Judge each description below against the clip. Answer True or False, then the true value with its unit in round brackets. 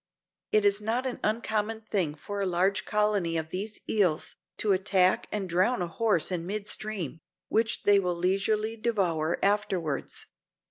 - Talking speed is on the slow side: False (155 wpm)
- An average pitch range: True (3.2 semitones)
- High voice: True (200 Hz)